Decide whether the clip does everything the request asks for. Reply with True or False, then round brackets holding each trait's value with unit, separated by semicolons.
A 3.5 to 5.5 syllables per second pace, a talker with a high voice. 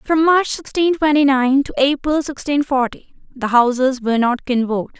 True (5.0 syllables/s; 270 Hz)